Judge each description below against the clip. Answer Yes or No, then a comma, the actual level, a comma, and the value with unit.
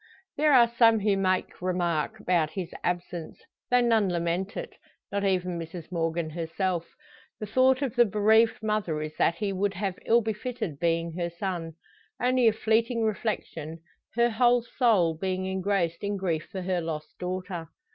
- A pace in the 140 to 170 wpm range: Yes, average, 165 wpm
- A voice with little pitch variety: No, average, 4.4 semitones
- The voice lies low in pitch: No, high, 190 Hz